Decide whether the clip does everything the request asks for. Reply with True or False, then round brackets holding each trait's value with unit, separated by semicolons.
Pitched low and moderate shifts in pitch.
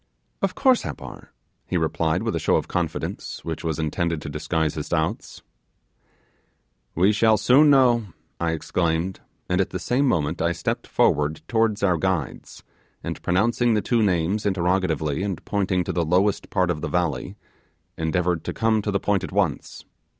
True (90 Hz; 4.4 semitones)